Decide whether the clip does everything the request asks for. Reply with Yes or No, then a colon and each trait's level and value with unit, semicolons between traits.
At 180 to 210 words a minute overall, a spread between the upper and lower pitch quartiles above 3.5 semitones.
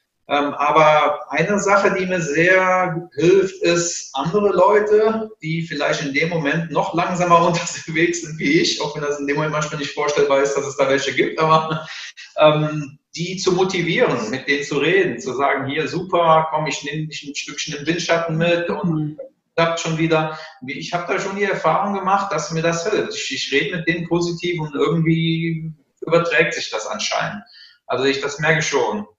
No: average, 185 wpm; average, 2.7 semitones